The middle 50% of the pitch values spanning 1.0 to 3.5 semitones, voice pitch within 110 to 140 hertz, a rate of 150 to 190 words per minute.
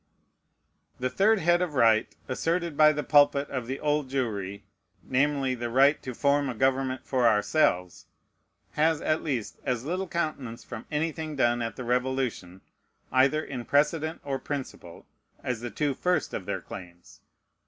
No: average, 4.0 semitones; low, 135 Hz; average, 155 wpm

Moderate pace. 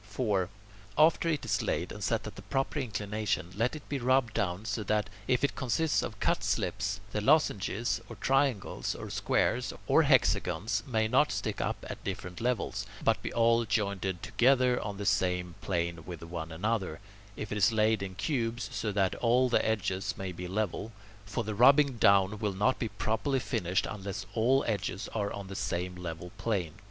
Yes: average, 185 wpm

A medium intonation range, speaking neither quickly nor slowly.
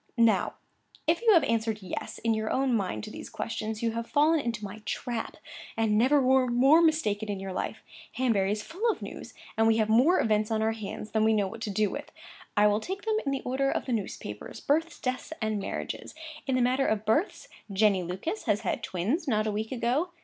No: average, 4.1 semitones; fast, 220 wpm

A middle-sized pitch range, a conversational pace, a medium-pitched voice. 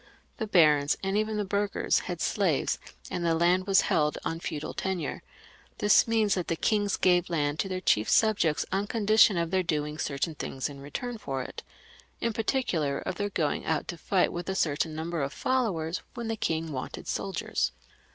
Yes: average, 5.0 semitones; average, 190 wpm; medium, 175 Hz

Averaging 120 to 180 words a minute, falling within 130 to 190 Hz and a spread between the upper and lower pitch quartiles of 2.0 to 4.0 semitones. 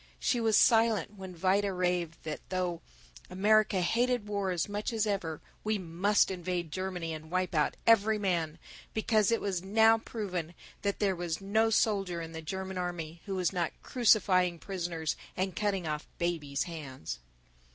Yes: average, 160 wpm; medium, 185 Hz; average, 3.4 semitones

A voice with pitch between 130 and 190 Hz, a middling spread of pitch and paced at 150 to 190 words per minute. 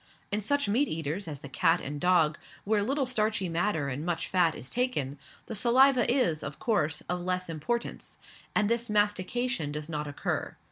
No: medium, 185 Hz; wide, 7.3 semitones; average, 180 wpm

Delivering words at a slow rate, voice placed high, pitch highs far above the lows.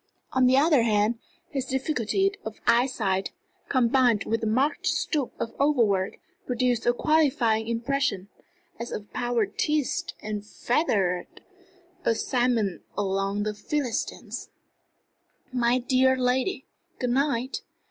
No: slow, 115 wpm; high, 240 Hz; average, 3.5 semitones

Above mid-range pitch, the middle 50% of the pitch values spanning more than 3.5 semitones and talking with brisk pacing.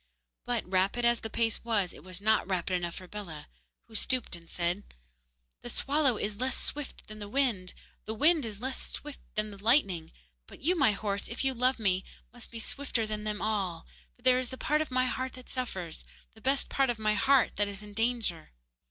Yes: high, 220 Hz; average, 4.4 semitones; fast, 215 wpm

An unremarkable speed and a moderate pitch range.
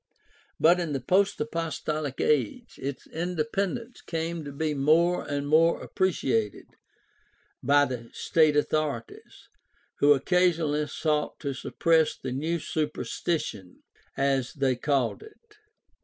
No: slow, 115 wpm; average, 3.3 semitones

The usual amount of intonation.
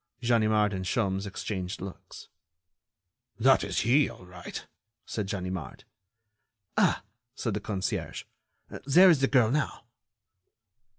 Yes: average, 4.3 semitones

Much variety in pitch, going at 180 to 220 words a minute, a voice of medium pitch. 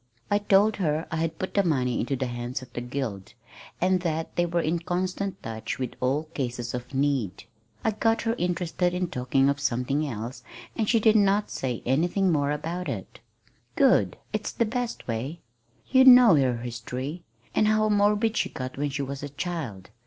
Yes: wide, 6.7 semitones; average, 190 wpm; medium, 155 Hz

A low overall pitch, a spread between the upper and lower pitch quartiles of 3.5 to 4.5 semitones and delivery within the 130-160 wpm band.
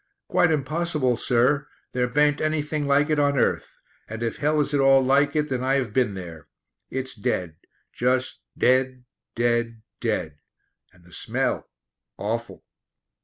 Yes: low, 130 Hz; average, 3.8 semitones; average, 150 wpm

